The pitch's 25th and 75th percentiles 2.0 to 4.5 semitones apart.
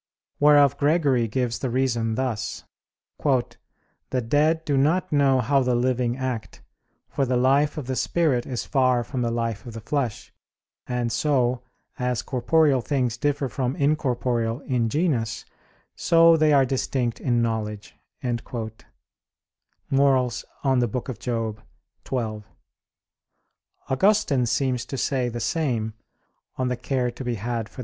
Yes: average, 2.8 semitones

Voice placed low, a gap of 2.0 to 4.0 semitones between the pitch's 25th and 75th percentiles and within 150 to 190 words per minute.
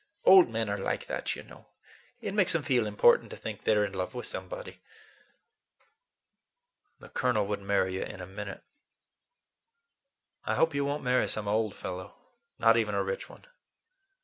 No: low, 105 Hz; average, 4.4 semitones; average, 170 wpm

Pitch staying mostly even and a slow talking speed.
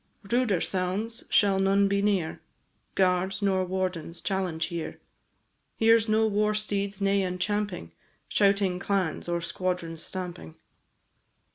Yes: narrow, 2.2 semitones; slow, 125 wpm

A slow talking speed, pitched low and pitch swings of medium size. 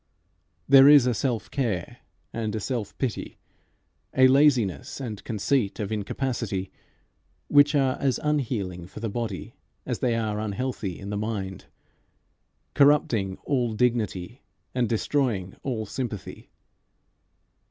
Yes: slow, 120 wpm; low, 115 Hz; average, 4.5 semitones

